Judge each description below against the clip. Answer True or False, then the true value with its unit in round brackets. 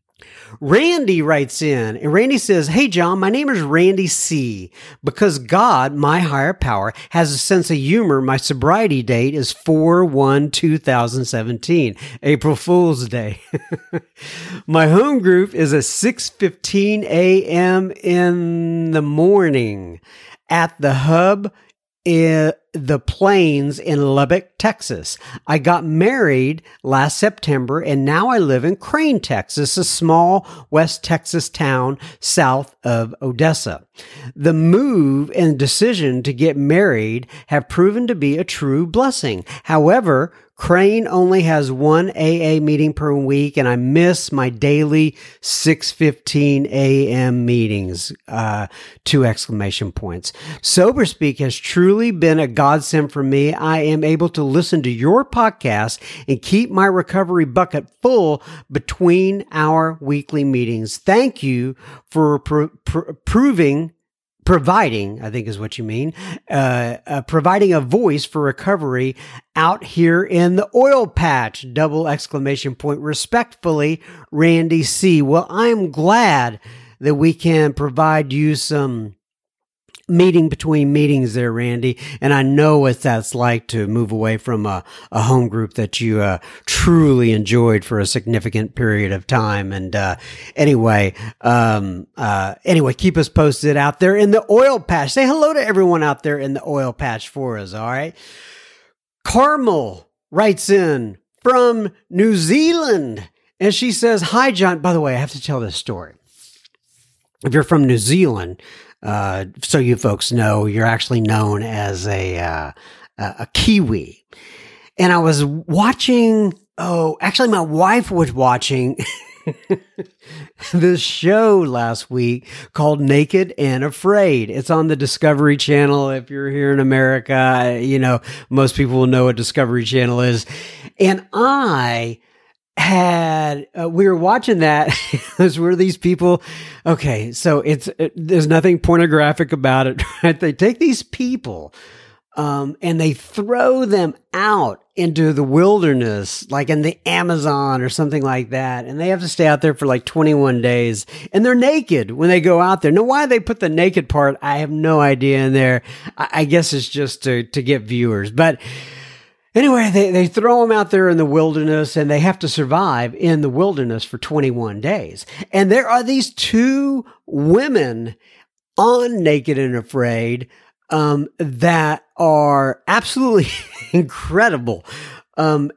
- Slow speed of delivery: False (150 wpm)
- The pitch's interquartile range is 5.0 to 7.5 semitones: True (5.4 semitones)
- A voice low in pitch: False (150 Hz)